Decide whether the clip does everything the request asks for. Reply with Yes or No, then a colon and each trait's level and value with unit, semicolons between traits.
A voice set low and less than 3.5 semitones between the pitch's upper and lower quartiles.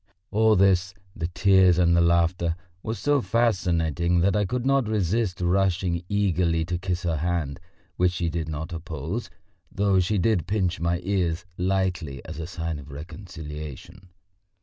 Yes: very low, 90 Hz; average, 2.8 semitones